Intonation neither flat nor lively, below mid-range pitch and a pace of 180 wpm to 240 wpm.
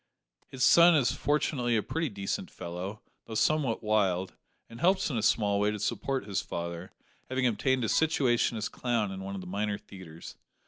Yes: average, 5.0 semitones; low, 110 Hz; average, 185 wpm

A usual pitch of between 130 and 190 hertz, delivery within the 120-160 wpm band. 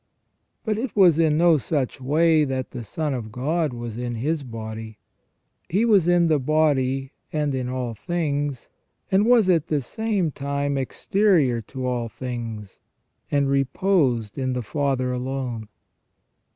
Yes: medium, 140 Hz; average, 150 wpm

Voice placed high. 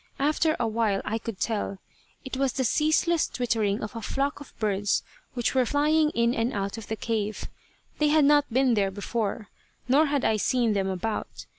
Yes: high, 235 Hz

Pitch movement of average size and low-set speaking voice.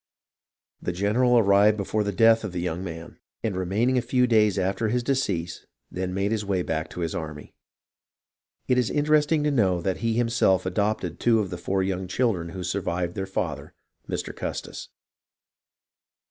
Yes: average, 4.1 semitones; low, 100 Hz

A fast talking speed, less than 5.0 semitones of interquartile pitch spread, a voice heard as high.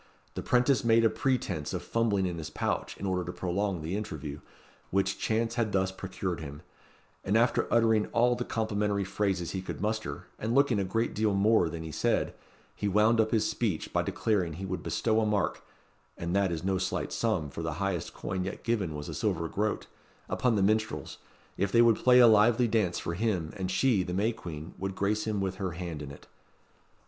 No: fast, 210 wpm; average, 3.8 semitones; low, 100 Hz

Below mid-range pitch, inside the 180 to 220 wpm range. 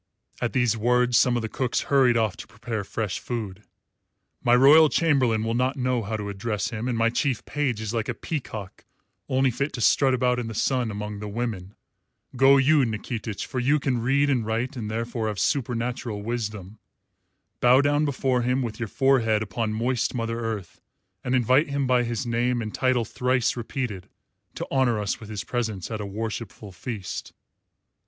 Yes: low, 120 Hz; average, 185 wpm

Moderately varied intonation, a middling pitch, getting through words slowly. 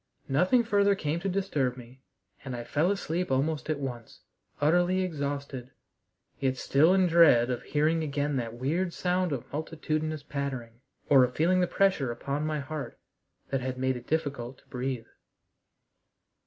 No: average, 4.3 semitones; medium, 145 Hz; average, 155 wpm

